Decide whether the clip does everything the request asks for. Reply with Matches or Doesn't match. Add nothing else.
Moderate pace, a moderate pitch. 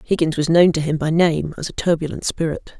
Doesn't match